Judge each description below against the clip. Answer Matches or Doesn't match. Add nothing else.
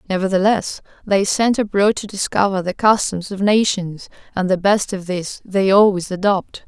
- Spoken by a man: Doesn't match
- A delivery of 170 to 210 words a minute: Doesn't match